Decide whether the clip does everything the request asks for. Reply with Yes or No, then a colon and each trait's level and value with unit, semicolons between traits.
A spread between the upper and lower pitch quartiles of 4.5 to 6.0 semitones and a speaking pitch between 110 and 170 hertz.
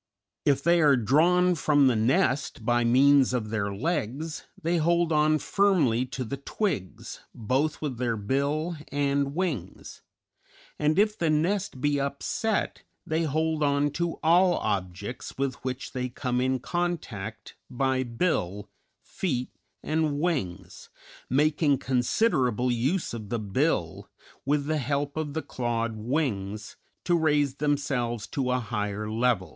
Yes: average, 4.8 semitones; medium, 140 Hz